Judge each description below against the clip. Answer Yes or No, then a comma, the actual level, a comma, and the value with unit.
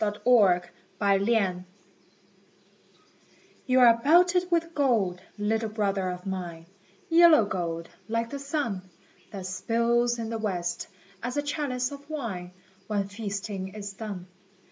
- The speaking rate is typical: No, slow, 125 wpm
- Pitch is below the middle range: No, high, 215 Hz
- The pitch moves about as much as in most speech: Yes, average, 4.8 semitones